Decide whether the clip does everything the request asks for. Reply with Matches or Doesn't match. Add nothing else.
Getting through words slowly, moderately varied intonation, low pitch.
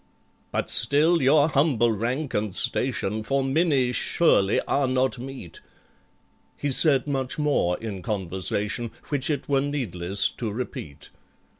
Matches